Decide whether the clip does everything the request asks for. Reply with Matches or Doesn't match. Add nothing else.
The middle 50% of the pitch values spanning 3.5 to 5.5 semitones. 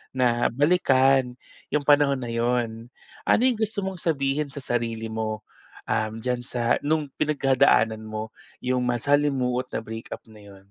Matches